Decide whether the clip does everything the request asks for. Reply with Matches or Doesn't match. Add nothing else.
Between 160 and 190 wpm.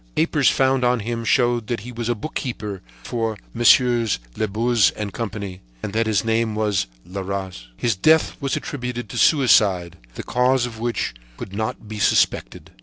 Matches